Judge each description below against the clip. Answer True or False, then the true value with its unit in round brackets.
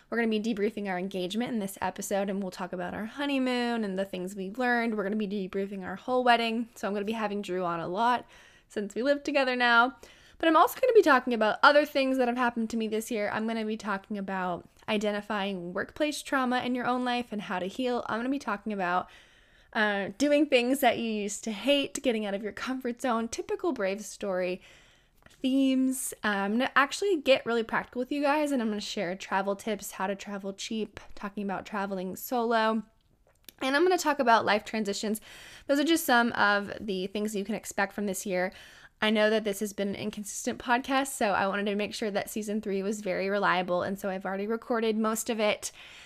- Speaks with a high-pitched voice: True (215 Hz)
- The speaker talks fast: True (230 wpm)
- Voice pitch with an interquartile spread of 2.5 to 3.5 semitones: False (3.9 semitones)